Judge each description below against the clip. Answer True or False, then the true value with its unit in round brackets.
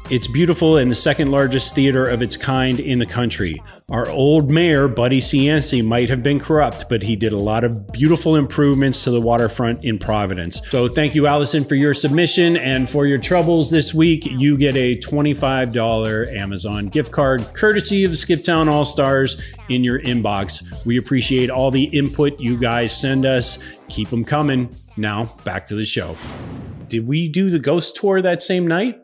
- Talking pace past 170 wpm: True (185 wpm)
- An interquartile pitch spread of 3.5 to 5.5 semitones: True (4.2 semitones)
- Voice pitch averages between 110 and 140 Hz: True (135 Hz)